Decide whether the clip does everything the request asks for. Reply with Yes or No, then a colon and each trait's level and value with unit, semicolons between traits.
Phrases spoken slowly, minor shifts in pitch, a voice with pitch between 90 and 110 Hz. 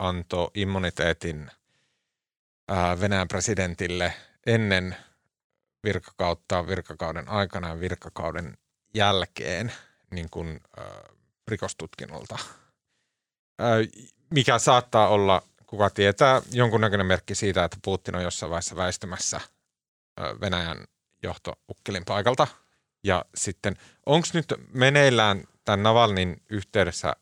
No: slow, 85 wpm; average, 3.5 semitones; very low, 95 Hz